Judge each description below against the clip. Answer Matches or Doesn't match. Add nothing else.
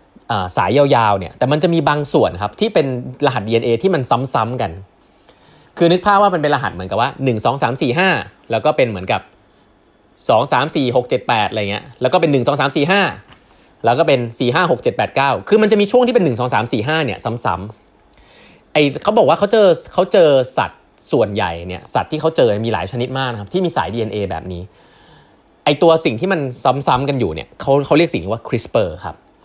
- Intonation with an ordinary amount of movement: Doesn't match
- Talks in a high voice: Doesn't match